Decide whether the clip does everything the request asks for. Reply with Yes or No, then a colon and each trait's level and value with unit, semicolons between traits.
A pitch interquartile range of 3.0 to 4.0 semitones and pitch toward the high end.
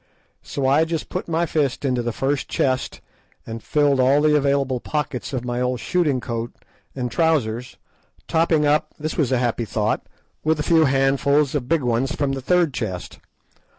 No: average, 3.3 semitones; low, 135 Hz